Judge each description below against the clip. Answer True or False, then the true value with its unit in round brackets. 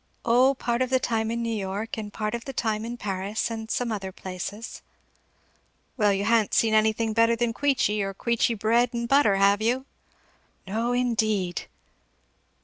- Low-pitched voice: False (225 Hz)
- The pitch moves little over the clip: True (2.2 semitones)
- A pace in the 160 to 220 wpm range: True (170 wpm)